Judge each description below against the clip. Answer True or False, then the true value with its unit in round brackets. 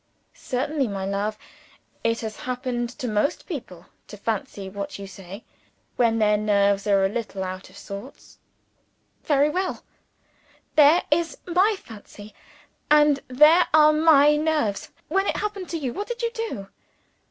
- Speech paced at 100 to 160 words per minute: True (150 wpm)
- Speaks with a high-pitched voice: True (245 Hz)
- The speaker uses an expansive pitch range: True (7.3 semitones)